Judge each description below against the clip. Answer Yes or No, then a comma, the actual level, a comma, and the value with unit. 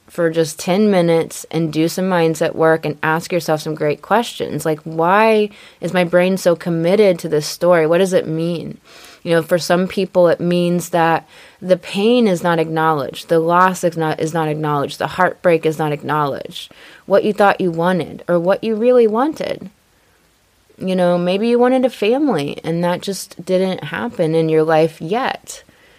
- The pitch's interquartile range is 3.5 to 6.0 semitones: No, average, 2.7 semitones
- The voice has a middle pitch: Yes, medium, 175 Hz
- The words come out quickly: No, average, 185 wpm